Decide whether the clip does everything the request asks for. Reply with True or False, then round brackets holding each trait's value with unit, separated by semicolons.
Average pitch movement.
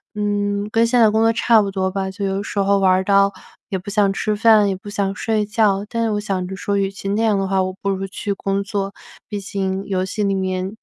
False (1.4 semitones)